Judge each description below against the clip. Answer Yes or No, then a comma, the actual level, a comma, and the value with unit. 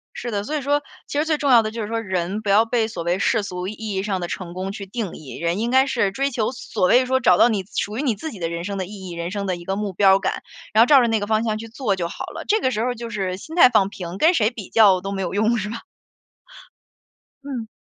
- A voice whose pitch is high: Yes, high, 210 Hz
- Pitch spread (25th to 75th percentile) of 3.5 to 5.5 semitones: Yes, average, 3.9 semitones